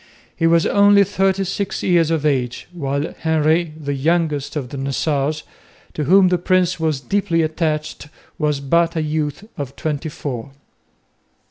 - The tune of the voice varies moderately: Yes, average, 3.3 semitones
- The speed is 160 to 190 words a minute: No, average, 150 wpm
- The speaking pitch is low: No, medium, 155 Hz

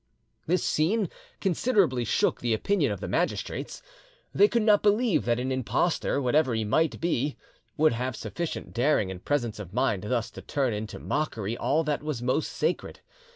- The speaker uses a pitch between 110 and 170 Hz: Yes, medium, 140 Hz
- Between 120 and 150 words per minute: No, average, 170 wpm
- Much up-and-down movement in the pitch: Yes, wide, 5.7 semitones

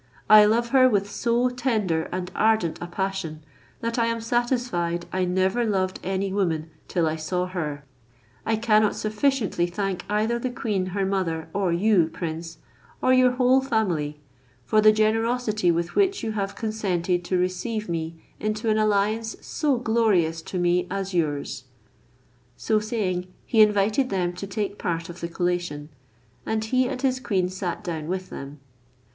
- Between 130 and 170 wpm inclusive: Yes, average, 165 wpm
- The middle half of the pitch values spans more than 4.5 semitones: No, average, 4.2 semitones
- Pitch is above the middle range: Yes, high, 195 Hz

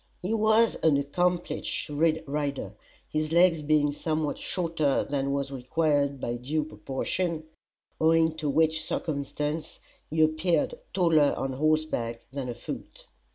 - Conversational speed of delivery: No, slow, 120 wpm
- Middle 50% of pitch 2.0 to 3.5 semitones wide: Yes, narrow, 2.5 semitones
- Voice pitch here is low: No, medium, 155 Hz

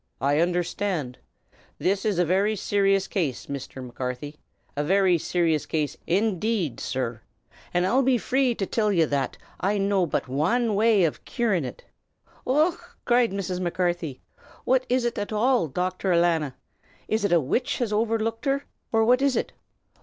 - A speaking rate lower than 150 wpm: No, average, 165 wpm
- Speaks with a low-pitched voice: No, high, 190 Hz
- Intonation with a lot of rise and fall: Yes, wide, 5.8 semitones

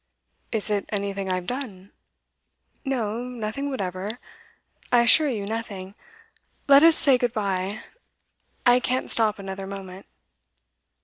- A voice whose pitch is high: Yes, high, 215 Hz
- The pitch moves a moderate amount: Yes, average, 4.1 semitones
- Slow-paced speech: Yes, slow, 120 wpm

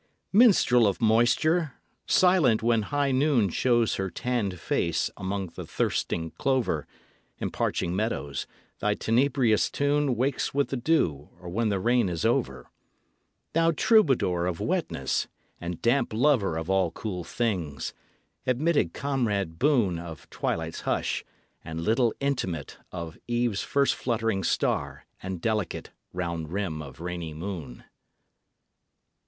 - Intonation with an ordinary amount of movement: No, wide, 6.9 semitones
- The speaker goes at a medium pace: No, slow, 130 wpm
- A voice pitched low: Yes, low, 110 Hz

